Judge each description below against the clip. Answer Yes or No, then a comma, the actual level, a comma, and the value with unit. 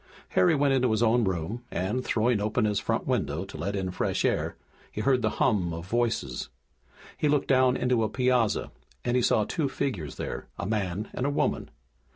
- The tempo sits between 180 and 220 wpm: Yes, average, 200 wpm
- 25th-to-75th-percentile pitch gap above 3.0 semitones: Yes, average, 4.5 semitones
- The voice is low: Yes, low, 110 Hz